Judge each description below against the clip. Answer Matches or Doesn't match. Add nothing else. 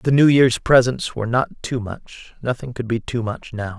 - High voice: Doesn't match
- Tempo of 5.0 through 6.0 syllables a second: Doesn't match